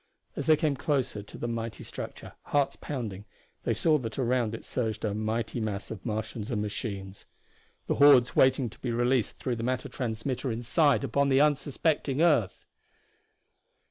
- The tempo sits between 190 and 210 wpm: No, average, 165 wpm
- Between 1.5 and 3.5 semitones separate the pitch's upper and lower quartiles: No, average, 4.0 semitones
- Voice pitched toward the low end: Yes, low, 120 Hz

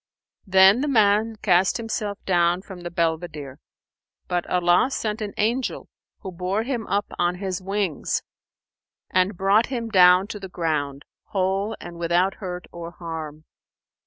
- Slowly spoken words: No, average, 150 wpm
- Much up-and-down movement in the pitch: No, average, 3.1 semitones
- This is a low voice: No, medium, 185 Hz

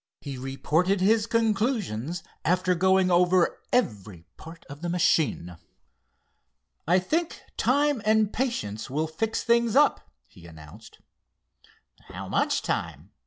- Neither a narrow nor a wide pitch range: No, wide, 7.6 semitones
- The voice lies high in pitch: No, medium, 180 Hz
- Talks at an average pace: No, slow, 120 wpm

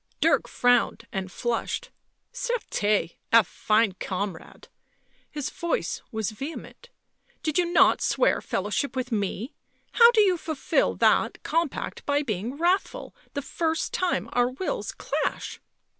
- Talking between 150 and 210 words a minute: No, average, 140 wpm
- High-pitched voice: Yes, very high, 270 Hz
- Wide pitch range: Yes, wide, 8.1 semitones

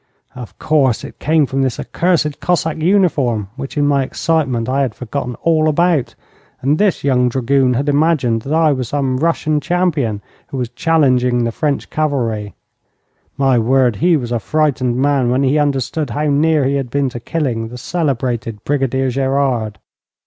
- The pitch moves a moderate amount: Yes, average, 3.7 semitones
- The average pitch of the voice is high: No, low, 135 Hz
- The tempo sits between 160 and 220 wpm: Yes, average, 170 wpm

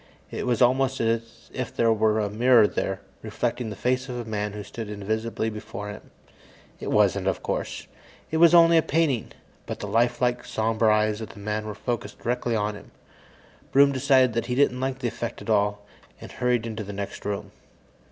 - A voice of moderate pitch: No, low, 115 Hz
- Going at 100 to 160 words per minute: No, average, 190 wpm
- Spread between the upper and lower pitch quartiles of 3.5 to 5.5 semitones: No, average, 2.8 semitones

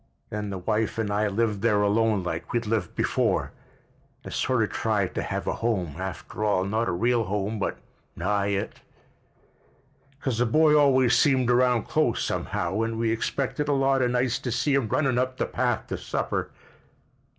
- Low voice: Yes, low, 115 Hz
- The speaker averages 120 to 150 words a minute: No, average, 180 wpm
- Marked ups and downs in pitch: No, average, 3.7 semitones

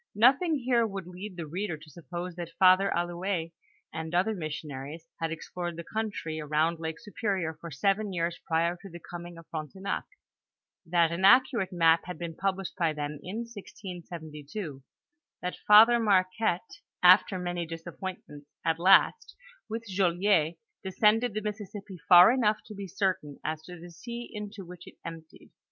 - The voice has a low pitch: No, medium, 180 Hz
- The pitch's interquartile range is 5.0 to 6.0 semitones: No, average, 3.6 semitones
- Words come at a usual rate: Yes, average, 155 wpm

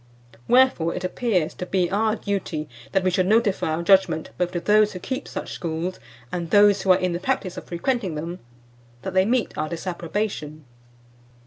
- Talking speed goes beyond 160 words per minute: Yes, average, 185 wpm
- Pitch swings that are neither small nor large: Yes, average, 3.3 semitones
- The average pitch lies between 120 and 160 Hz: No, medium, 185 Hz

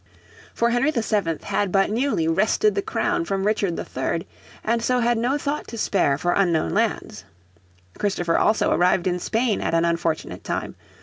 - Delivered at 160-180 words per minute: Yes, average, 170 wpm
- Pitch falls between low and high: No, high, 205 Hz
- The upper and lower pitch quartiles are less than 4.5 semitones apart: No, average, 5.1 semitones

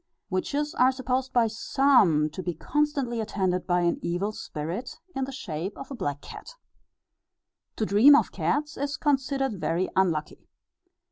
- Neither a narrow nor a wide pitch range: No, wide, 7.2 semitones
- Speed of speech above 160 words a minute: No, average, 150 wpm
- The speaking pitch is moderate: No, high, 230 Hz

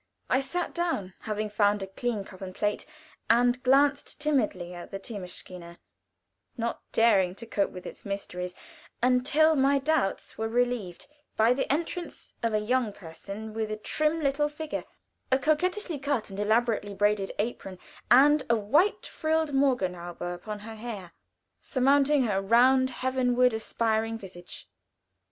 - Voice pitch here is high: Yes, high, 230 Hz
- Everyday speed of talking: Yes, average, 145 wpm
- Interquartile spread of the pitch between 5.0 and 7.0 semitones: Yes, average, 5.3 semitones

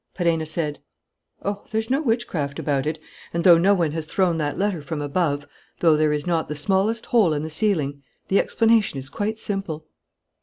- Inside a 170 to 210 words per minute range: Yes, average, 190 wpm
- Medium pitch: Yes, medium, 165 Hz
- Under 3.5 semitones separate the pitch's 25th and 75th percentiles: No, average, 5.1 semitones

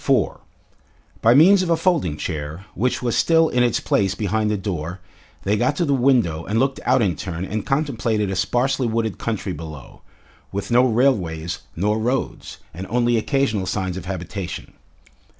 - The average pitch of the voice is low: Yes, low, 110 Hz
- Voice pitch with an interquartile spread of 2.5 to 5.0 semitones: No, wide, 5.4 semitones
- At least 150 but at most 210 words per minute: Yes, average, 170 wpm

